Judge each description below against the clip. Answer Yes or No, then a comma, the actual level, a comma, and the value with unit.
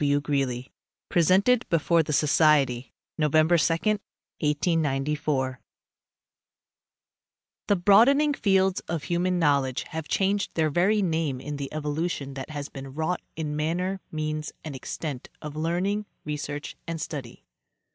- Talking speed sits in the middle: No, slow, 125 wpm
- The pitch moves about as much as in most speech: Yes, average, 3.5 semitones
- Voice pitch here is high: No, medium, 155 Hz